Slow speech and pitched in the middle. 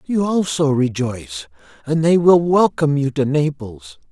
Yes: slow, 130 wpm; medium, 145 Hz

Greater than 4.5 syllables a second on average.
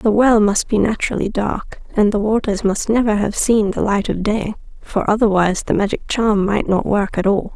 Yes: 5.1 syllables/s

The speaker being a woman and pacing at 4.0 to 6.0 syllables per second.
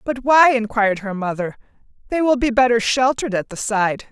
Yes: female; 5.4 syllables/s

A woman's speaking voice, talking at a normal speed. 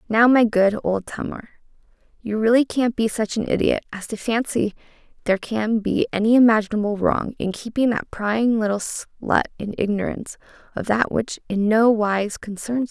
Yes: female; average, 170 wpm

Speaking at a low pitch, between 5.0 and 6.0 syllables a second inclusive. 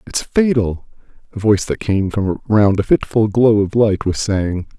No: low, 105 Hz; 4.5 syllables/s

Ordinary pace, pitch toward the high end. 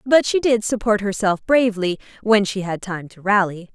Yes: average, 190 wpm; high, 205 Hz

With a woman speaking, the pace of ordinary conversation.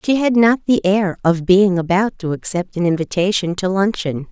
Yes: female; average, 195 wpm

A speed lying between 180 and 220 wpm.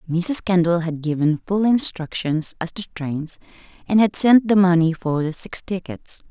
No: average, 170 wpm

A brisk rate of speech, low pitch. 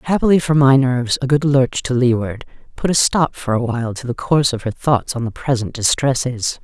Yes: fast, 225 wpm; low, 130 Hz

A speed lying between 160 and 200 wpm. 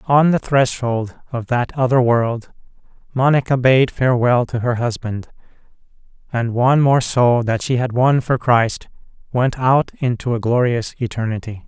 No: average, 150 wpm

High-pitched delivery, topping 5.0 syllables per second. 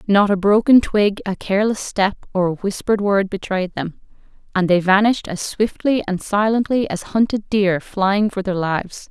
No: high, 200 Hz; 4.9 syllables/s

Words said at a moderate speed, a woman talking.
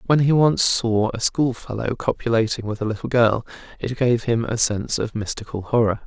No: average, 190 wpm; male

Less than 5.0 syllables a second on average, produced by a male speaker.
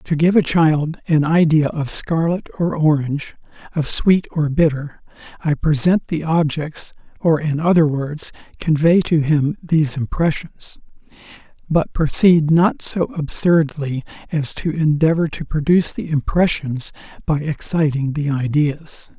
Yes: 4.2 syllables/s; male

